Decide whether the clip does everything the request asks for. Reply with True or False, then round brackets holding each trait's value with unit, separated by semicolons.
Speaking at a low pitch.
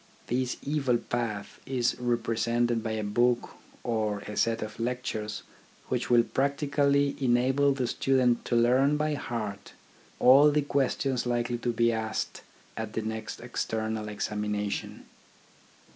True (120 Hz)